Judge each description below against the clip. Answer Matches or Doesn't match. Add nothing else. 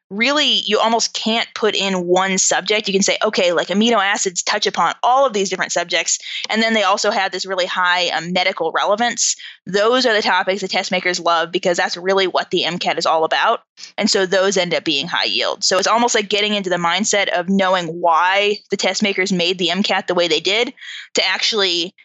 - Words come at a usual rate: Doesn't match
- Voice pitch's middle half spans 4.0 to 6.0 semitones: Doesn't match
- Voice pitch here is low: Doesn't match